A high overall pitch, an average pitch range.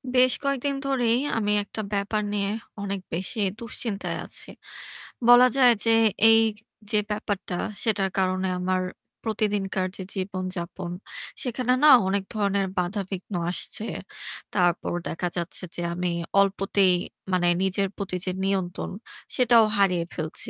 Yes: high, 200 Hz; average, 3.1 semitones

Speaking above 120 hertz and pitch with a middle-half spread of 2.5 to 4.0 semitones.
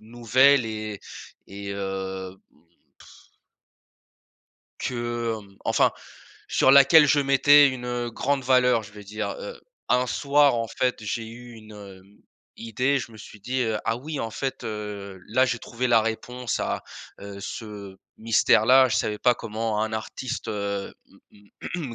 No: low, 115 Hz; average, 3.4 semitones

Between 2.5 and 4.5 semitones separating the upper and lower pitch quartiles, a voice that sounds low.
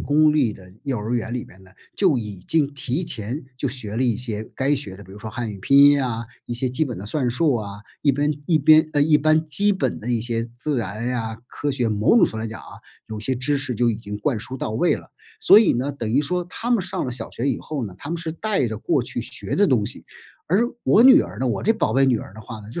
No: average, 5.2 semitones; low, 125 Hz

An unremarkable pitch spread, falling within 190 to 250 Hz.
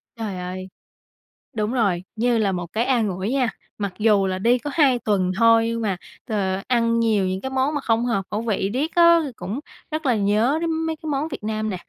Yes: average, 4.3 semitones; high, 225 Hz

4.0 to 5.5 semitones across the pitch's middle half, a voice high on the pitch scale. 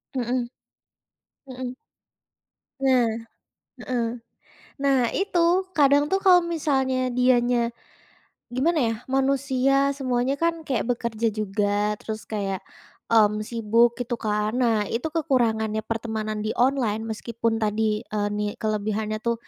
No: average, 3.6 semitones; high, 235 Hz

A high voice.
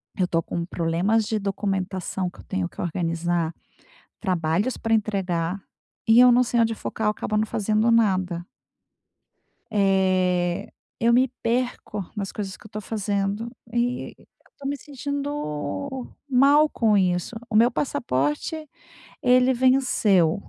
Yes: high, 210 Hz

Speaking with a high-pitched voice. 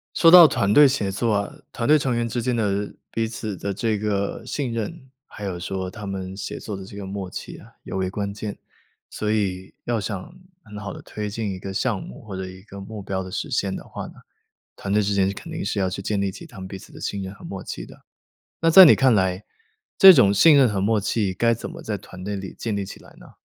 No: low, 100 Hz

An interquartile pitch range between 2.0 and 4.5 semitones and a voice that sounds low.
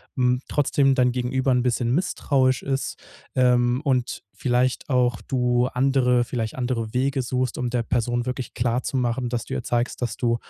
No: narrow, 1.2 semitones; low, 125 Hz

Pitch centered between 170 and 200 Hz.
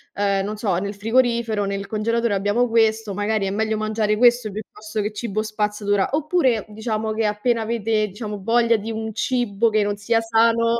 No: high, 215 Hz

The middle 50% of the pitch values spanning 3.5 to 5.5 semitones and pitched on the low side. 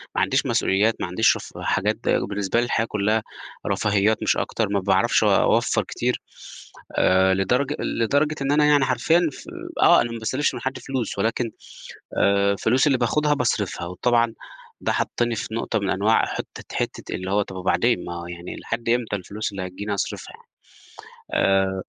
Yes: average, 3.8 semitones; low, 110 Hz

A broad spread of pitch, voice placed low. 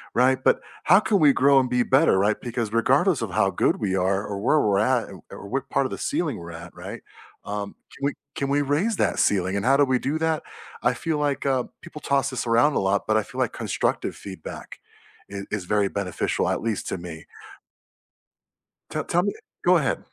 Yes: wide, 5.9 semitones; low, 125 Hz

